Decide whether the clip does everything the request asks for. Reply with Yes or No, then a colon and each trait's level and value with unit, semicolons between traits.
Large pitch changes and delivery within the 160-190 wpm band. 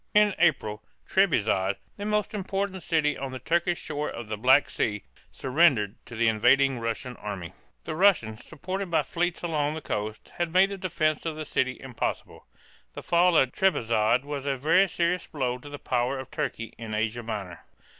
Yes: wide, 7.0 semitones; average, 180 wpm